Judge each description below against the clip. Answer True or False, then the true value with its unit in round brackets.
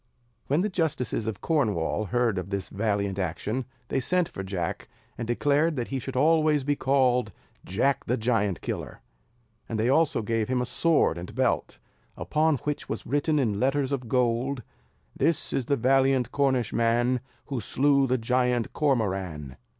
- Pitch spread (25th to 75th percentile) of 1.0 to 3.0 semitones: False (4.4 semitones)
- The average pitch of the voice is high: False (125 Hz)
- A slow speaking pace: False (160 wpm)